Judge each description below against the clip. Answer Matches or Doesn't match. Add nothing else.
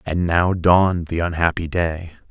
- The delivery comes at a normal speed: Matches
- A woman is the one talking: Doesn't match